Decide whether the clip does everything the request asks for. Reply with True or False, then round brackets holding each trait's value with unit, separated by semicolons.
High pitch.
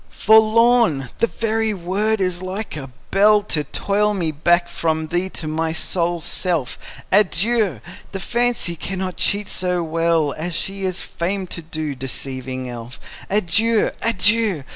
False (180 Hz)